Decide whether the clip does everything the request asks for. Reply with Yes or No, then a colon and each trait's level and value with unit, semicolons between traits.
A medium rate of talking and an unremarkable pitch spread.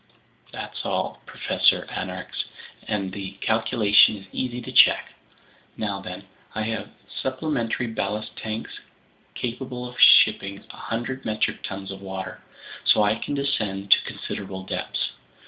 No: slow, 130 wpm; average, 3.8 semitones